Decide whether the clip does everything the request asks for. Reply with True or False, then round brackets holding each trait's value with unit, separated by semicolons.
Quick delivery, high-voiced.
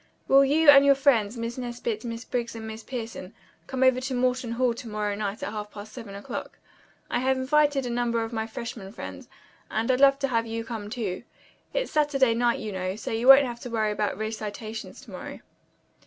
True (210 wpm; 235 Hz)